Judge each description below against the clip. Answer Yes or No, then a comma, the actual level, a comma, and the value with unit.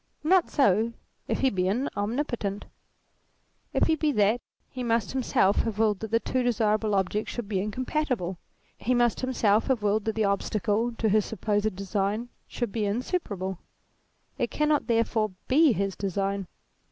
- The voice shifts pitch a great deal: No, average, 3.4 semitones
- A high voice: Yes, high, 220 Hz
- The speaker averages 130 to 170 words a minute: Yes, average, 165 wpm